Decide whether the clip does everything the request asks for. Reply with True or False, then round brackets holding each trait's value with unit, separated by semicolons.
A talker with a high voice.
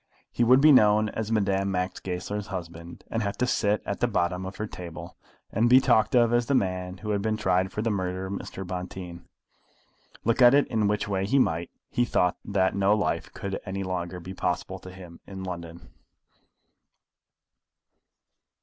False (95 Hz)